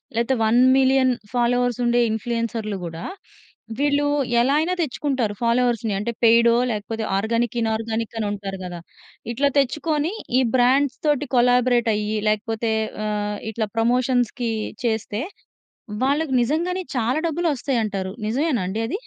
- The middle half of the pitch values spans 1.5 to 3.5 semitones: Yes, average, 3.2 semitones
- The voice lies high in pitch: Yes, high, 240 Hz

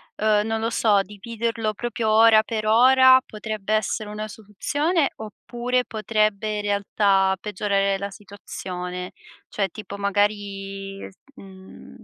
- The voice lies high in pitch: Yes, high, 210 Hz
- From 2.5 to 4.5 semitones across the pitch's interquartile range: No, narrow, 2.1 semitones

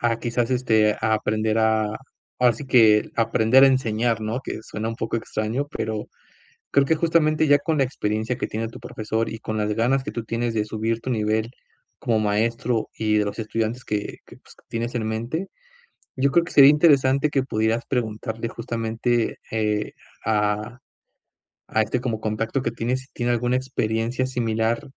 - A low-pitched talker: Yes, low, 115 Hz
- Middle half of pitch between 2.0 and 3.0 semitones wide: Yes, narrow, 2.6 semitones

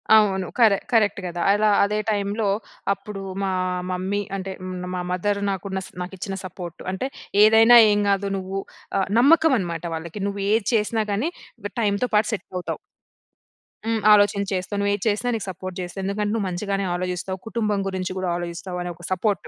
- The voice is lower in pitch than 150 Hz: No, high, 200 Hz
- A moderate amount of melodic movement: No, narrow, 2.2 semitones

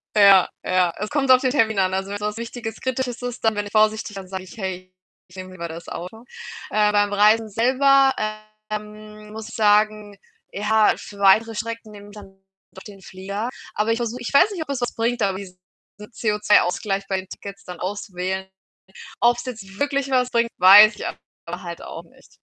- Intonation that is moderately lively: Yes, average, 3.0 semitones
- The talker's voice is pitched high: Yes, high, 210 Hz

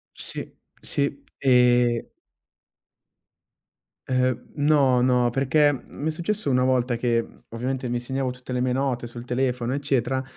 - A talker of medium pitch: No, low, 125 Hz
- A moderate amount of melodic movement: No, narrow, 1.9 semitones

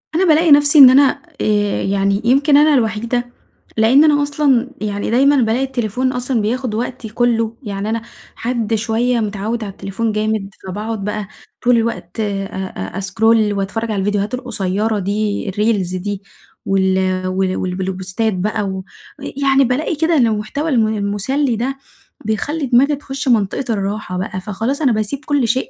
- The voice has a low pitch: No, high, 220 Hz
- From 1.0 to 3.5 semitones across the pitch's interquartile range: No, average, 4.3 semitones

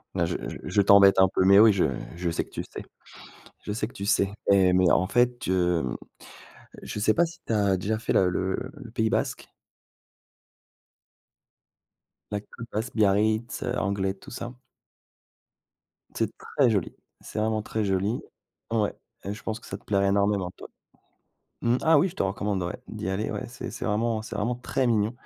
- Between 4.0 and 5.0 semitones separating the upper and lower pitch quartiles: No, average, 3.0 semitones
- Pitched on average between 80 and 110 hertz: Yes, low, 105 Hz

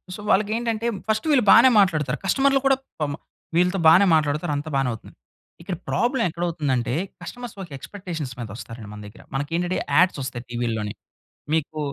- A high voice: No, medium, 165 Hz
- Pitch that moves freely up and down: Yes, wide, 7.6 semitones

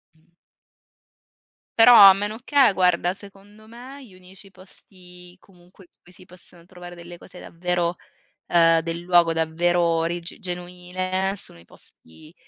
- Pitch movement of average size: No, narrow, 2.0 semitones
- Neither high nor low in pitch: Yes, medium, 180 Hz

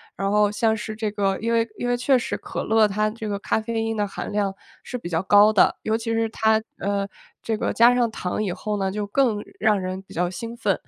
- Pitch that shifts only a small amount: Yes, narrow, 2.1 semitones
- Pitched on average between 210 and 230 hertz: Yes, high, 215 Hz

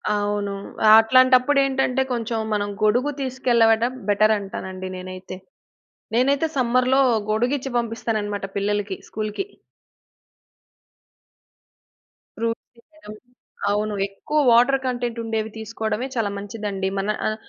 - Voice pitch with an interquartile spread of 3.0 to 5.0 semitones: Yes, average, 3.4 semitones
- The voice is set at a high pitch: Yes, high, 225 Hz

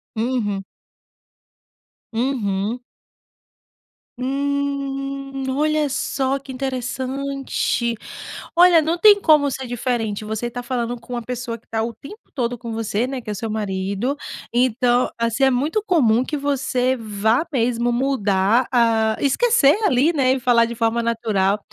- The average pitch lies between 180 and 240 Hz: No, very high, 250 Hz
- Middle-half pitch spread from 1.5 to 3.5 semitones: Yes, average, 3.2 semitones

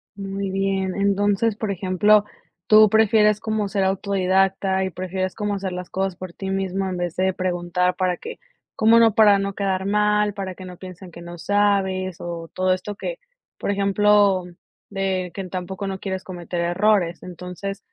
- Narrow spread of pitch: Yes, narrow, 1.7 semitones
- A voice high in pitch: Yes, high, 195 Hz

